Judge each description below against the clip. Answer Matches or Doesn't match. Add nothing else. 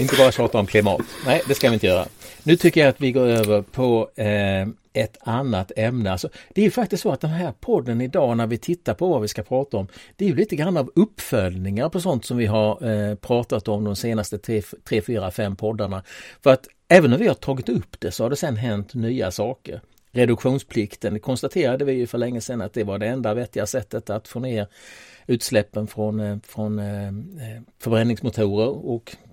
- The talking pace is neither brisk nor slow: Doesn't match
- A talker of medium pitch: Doesn't match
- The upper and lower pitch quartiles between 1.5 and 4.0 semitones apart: Matches